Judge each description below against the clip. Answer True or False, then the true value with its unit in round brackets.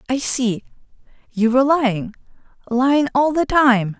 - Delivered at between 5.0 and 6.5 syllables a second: False (4.7 syllables/s)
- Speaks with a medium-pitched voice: False (250 Hz)